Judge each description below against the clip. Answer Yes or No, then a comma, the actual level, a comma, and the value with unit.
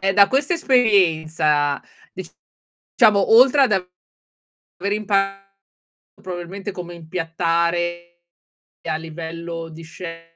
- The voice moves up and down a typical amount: Yes, average, 3.1 semitones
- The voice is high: No, medium, 175 Hz